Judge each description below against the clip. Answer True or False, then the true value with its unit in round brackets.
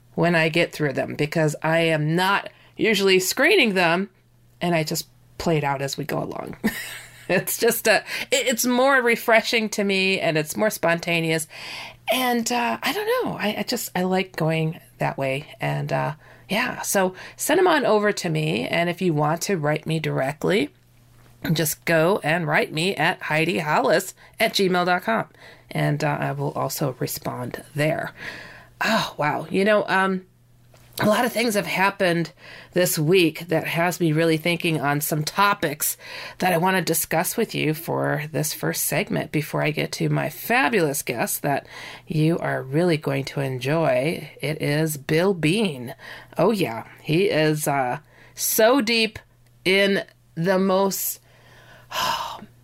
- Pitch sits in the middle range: True (165 Hz)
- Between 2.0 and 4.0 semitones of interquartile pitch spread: False (4.4 semitones)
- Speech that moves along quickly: False (165 wpm)